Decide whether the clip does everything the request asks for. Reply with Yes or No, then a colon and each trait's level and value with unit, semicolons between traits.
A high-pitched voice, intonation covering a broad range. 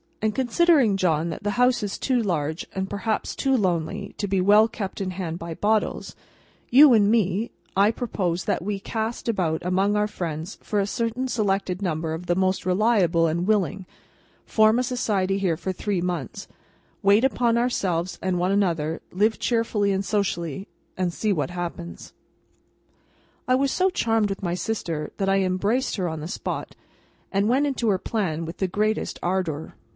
No: high, 195 Hz; average, 3.9 semitones